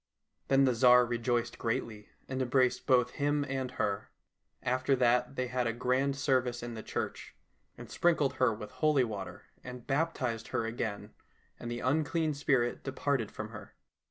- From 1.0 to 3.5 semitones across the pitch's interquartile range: Yes, narrow, 2.5 semitones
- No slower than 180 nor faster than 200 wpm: No, average, 160 wpm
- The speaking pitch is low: Yes, low, 125 Hz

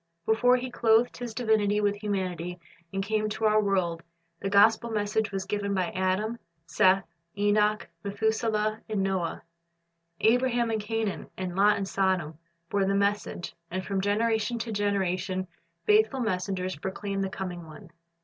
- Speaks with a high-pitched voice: Yes, high, 205 Hz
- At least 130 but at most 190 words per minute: Yes, average, 150 wpm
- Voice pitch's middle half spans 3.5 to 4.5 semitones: No, narrow, 2.5 semitones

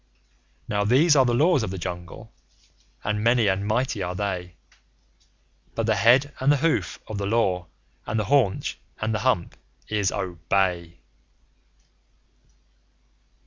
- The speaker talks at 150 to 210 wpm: No, average, 140 wpm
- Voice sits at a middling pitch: No, low, 105 Hz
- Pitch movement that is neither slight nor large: Yes, average, 4.7 semitones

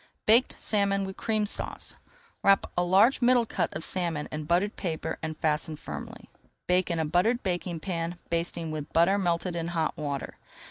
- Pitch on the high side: No, medium, 175 Hz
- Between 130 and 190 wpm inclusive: Yes, average, 175 wpm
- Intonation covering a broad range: No, average, 3.4 semitones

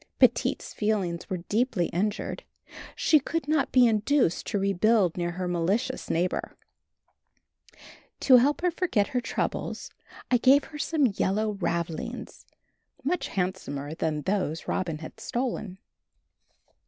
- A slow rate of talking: Yes, slow, 125 wpm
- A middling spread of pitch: No, wide, 6.5 semitones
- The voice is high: Yes, high, 205 Hz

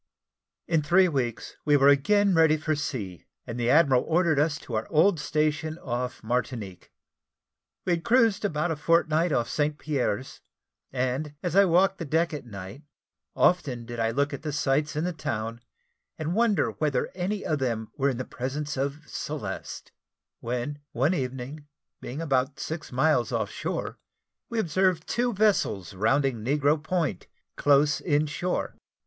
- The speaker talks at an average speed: Yes, average, 160 wpm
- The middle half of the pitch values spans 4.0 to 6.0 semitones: Yes, average, 4.4 semitones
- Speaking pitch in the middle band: Yes, medium, 145 Hz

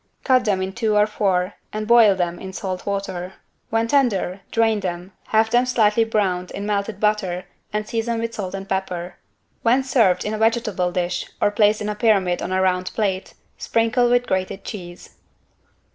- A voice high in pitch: Yes, high, 205 Hz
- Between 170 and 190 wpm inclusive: Yes, average, 180 wpm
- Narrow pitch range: No, average, 3.2 semitones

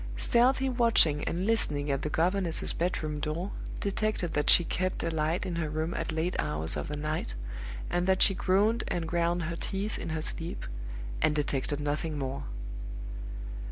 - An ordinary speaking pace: Yes, average, 170 wpm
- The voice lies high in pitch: No, medium, 165 Hz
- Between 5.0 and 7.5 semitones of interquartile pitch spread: No, average, 3.6 semitones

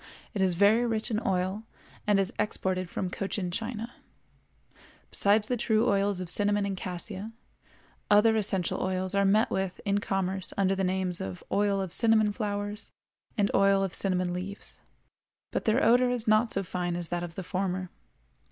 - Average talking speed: Yes, average, 170 wpm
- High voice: Yes, high, 195 Hz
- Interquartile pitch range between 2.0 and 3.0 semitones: Yes, narrow, 2.5 semitones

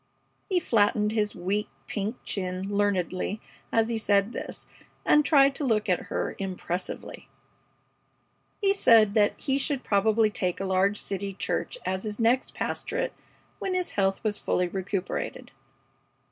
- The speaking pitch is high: Yes, high, 210 Hz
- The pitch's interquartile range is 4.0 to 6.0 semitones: No, average, 3.5 semitones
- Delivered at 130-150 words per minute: Yes, average, 145 wpm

